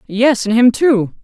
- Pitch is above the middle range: Yes, high, 235 Hz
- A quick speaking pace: No, average, 195 wpm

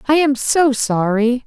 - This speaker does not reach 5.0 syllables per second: Yes, 3.8 syllables/s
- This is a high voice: Yes, very high, 255 Hz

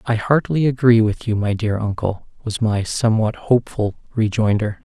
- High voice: No, low, 110 Hz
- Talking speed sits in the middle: Yes, average, 155 wpm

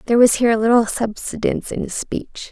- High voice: Yes, high, 230 Hz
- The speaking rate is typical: No, fast, 215 wpm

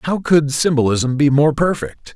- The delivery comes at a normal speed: Yes, average, 165 wpm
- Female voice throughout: No, male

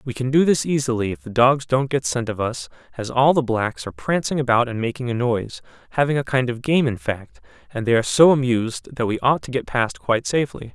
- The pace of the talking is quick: Yes, fast, 245 wpm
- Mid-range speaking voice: No, low, 125 Hz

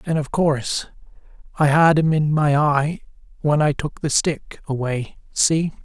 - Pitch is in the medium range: Yes, medium, 150 Hz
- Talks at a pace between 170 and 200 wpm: No, average, 155 wpm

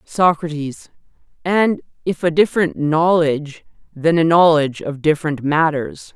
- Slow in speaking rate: Yes, slow, 115 wpm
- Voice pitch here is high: No, medium, 160 Hz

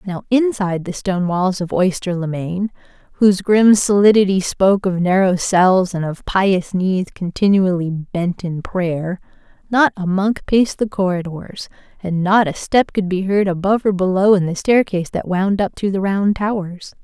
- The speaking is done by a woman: Yes, female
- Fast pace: No, average, 175 wpm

